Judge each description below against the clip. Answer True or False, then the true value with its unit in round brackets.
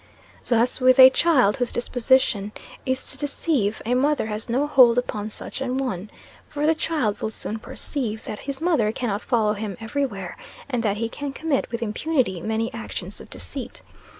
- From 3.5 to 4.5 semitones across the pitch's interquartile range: True (4.0 semitones)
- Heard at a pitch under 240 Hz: False (245 Hz)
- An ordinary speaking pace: True (180 wpm)